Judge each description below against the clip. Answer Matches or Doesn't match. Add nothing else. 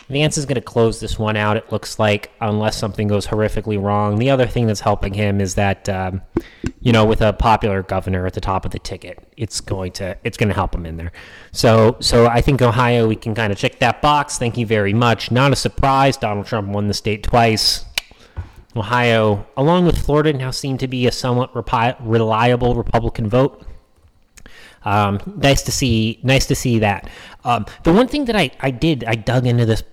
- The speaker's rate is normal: Doesn't match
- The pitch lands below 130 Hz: Matches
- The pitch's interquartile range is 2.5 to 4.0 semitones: Matches